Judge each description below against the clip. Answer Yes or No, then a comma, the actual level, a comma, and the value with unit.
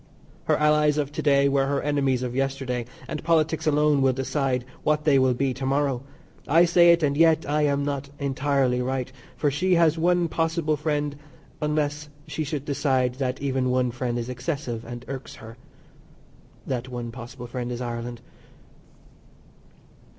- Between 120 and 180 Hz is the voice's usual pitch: Yes, medium, 140 Hz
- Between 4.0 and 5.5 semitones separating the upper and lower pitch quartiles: No, average, 3.0 semitones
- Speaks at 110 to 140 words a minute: No, average, 165 wpm